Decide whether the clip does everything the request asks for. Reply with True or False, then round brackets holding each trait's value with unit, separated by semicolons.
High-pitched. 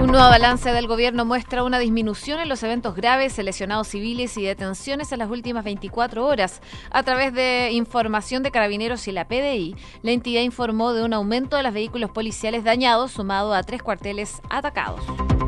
True (235 Hz)